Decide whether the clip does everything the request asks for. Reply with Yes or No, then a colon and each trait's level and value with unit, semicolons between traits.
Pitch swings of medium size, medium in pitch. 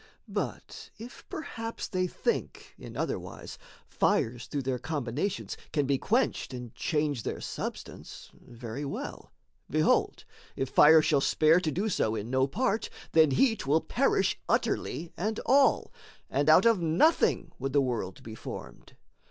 No: wide, 6.9 semitones; medium, 150 Hz